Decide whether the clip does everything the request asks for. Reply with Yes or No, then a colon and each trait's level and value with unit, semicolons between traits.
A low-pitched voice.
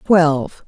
No: medium, 160 Hz